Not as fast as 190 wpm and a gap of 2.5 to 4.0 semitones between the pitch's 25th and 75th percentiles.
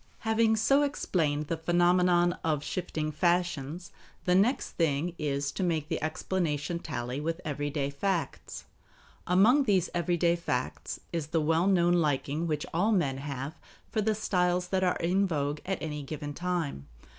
Yes: average, 155 wpm; average, 3.5 semitones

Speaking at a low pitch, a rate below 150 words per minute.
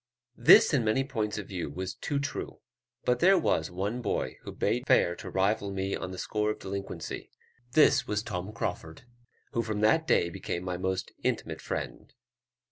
No: low, 105 Hz; average, 180 wpm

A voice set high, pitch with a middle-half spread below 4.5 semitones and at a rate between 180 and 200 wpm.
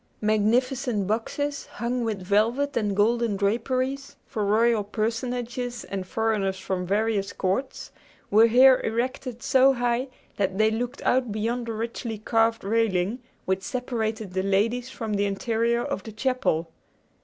No: high, 225 Hz; average, 3.2 semitones; average, 140 wpm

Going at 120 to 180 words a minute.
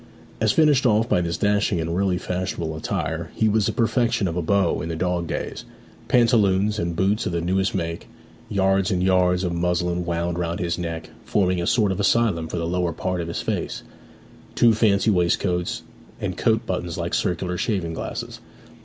No: average, 190 wpm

